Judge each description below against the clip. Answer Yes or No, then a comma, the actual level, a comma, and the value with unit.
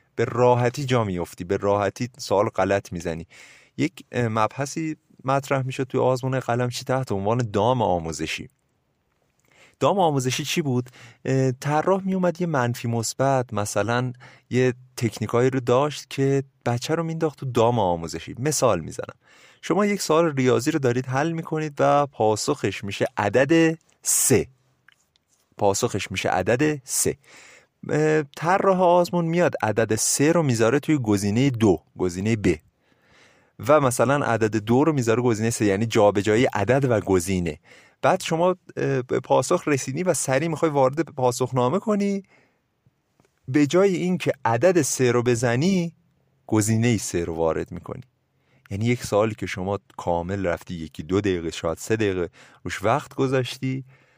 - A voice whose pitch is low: Yes, low, 125 Hz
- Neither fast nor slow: Yes, average, 145 wpm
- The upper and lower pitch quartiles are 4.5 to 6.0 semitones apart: Yes, average, 5.2 semitones